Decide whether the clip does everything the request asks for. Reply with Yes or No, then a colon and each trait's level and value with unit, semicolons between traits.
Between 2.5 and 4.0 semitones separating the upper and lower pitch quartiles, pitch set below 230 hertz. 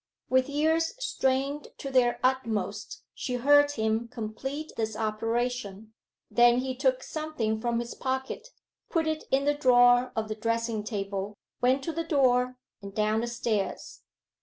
No: average, 3.5 semitones; high, 245 Hz